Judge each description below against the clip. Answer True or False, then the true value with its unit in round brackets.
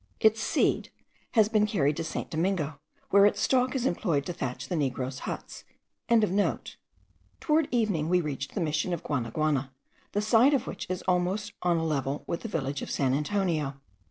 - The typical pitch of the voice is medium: True (170 Hz)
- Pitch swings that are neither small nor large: False (6.4 semitones)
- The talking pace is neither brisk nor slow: True (175 wpm)